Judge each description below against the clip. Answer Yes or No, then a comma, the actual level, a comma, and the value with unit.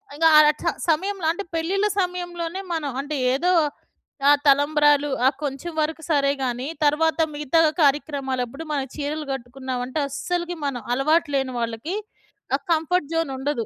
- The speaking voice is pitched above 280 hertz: Yes, very high, 295 Hz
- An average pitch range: Yes, average, 3.3 semitones